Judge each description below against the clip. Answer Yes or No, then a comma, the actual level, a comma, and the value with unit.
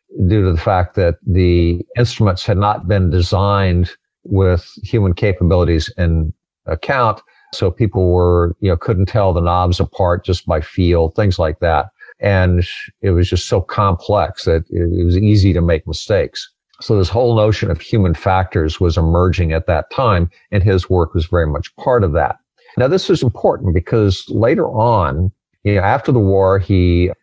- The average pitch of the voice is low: Yes, very low, 95 Hz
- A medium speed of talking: Yes, average, 175 wpm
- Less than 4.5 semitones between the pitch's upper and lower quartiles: Yes, average, 2.8 semitones